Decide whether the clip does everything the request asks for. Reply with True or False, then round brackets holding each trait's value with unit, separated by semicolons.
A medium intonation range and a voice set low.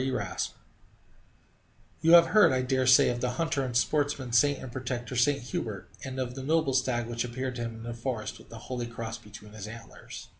False (2.2 semitones; 125 Hz)